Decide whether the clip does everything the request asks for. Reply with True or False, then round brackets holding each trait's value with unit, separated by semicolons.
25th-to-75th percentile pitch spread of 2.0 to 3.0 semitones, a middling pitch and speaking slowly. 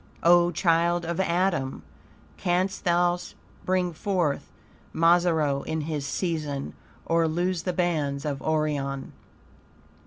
True (2.6 semitones; 170 Hz; 105 wpm)